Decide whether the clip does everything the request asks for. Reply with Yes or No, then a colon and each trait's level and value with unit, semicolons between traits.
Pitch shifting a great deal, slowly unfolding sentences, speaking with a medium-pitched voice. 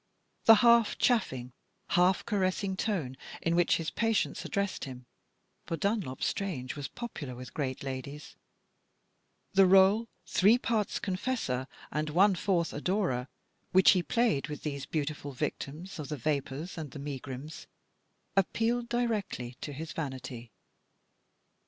Yes: wide, 6.5 semitones; slow, 130 wpm; medium, 165 Hz